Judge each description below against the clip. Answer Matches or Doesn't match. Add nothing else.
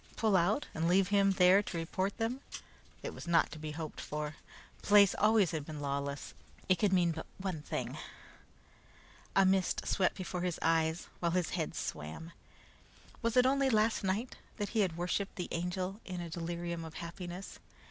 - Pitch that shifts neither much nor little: Matches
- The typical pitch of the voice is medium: Matches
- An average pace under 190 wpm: Matches